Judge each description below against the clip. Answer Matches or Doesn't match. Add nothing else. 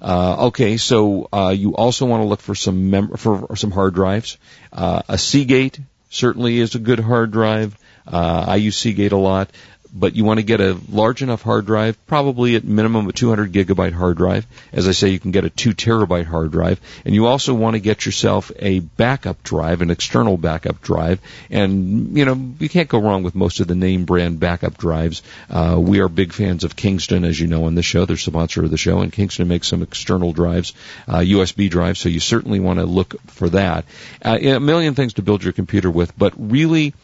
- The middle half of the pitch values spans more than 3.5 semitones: Matches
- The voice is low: Matches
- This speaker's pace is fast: Matches